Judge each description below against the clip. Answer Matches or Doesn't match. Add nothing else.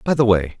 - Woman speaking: Doesn't match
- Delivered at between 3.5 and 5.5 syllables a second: Doesn't match